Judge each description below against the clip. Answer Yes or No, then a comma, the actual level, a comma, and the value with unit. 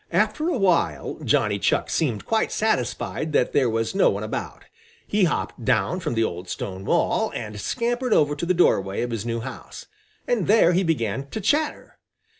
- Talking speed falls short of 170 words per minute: No, average, 185 wpm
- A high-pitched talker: No, medium, 145 Hz